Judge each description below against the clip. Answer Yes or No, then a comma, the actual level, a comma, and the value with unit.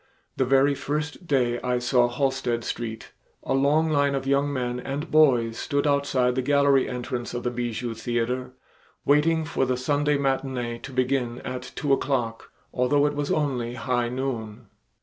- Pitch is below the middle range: Yes, low, 130 Hz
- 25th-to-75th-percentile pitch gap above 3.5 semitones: No, narrow, 2.6 semitones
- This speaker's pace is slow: No, average, 165 wpm